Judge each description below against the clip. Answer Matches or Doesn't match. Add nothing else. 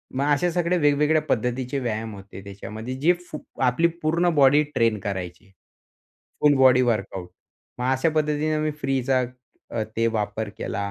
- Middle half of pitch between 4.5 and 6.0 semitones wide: Matches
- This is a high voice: Doesn't match